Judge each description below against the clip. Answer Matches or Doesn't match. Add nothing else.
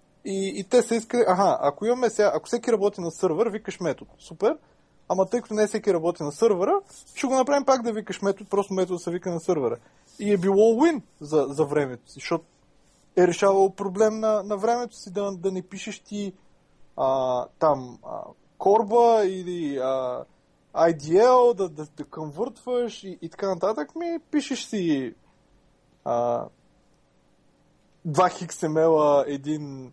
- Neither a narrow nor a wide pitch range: Doesn't match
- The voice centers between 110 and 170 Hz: Doesn't match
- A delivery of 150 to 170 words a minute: Matches